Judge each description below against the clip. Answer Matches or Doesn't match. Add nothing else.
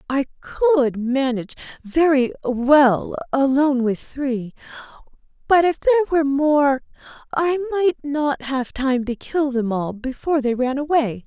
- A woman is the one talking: Matches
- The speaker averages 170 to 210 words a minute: Doesn't match